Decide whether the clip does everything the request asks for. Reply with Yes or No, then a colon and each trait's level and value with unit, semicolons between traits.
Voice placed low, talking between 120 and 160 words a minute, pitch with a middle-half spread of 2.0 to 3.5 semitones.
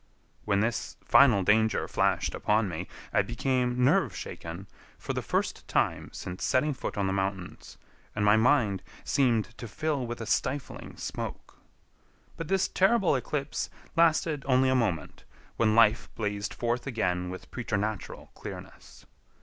No: low, 115 Hz; average, 145 wpm; average, 4.5 semitones